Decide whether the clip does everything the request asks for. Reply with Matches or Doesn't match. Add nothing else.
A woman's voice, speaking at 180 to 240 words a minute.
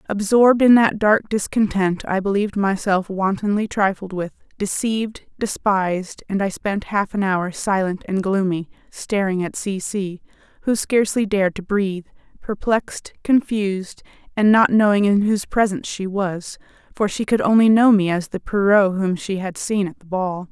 Doesn't match